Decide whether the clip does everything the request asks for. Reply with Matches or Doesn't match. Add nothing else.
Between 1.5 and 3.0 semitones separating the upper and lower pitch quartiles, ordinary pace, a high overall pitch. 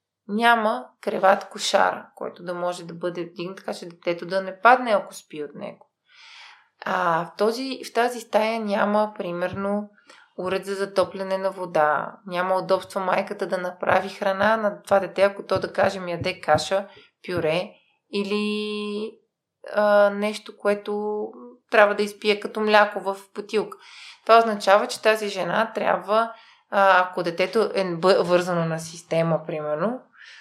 Matches